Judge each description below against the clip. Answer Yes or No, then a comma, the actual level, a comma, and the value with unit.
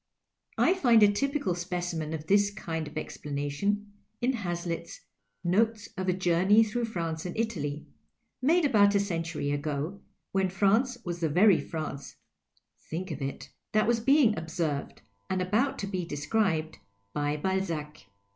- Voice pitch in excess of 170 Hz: Yes, medium, 185 Hz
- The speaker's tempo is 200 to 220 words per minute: No, average, 155 wpm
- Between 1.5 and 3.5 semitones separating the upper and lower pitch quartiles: No, average, 4.8 semitones